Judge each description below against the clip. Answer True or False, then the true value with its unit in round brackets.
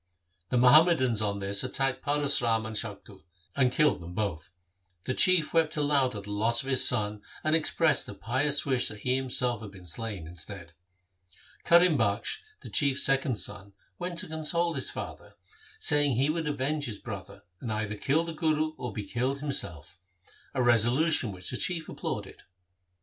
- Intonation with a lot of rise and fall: True (6.3 semitones)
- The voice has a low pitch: True (125 Hz)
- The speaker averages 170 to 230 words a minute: True (175 wpm)